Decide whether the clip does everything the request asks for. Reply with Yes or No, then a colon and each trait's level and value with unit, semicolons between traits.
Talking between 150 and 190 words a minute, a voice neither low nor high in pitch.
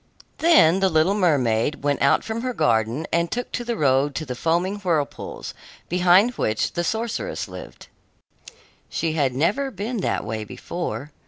Yes: average, 155 wpm; medium, 170 Hz